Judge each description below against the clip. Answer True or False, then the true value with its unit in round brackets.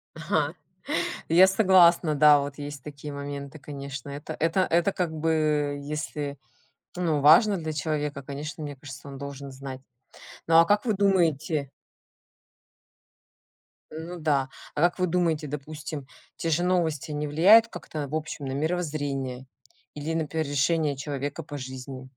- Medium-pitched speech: True (150 Hz)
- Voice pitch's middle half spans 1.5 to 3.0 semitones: True (2.7 semitones)